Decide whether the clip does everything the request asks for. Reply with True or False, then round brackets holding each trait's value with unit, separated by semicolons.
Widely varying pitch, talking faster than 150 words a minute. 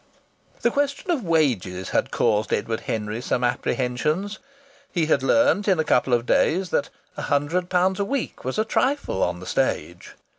True (8.8 semitones; 175 wpm)